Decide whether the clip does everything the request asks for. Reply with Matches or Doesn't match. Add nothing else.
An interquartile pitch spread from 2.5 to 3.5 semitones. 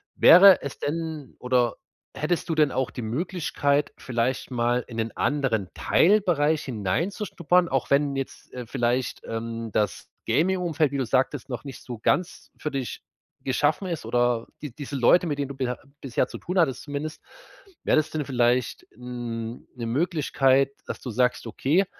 Doesn't match